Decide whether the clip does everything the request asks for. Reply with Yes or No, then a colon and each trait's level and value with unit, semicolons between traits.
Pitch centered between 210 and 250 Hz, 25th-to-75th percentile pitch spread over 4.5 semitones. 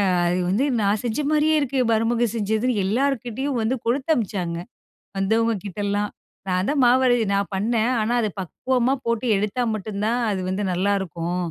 No: high, 220 Hz; average, 3.7 semitones